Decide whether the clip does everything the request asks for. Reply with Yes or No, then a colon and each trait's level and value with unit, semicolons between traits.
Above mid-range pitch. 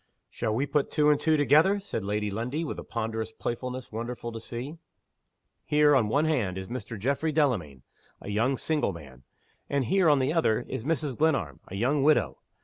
No: low, 130 Hz